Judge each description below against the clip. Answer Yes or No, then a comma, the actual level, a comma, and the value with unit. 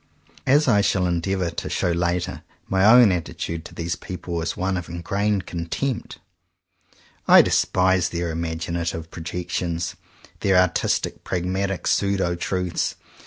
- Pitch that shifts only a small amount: Yes, narrow, 2.2 semitones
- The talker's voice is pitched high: No, very low, 90 Hz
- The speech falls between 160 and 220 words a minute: No, slow, 135 wpm